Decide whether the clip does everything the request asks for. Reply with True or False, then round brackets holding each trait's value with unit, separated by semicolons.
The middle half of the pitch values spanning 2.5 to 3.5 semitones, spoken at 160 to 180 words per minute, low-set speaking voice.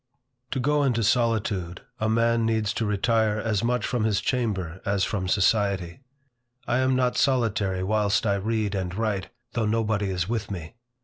True (2.9 semitones; 170 wpm; 110 Hz)